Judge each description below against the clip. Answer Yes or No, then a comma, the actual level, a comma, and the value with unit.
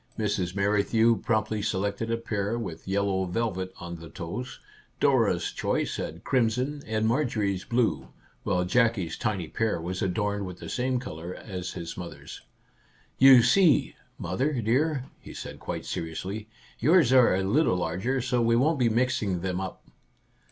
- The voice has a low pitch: Yes, low, 110 Hz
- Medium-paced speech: Yes, average, 160 wpm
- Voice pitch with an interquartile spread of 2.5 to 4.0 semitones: No, average, 4.8 semitones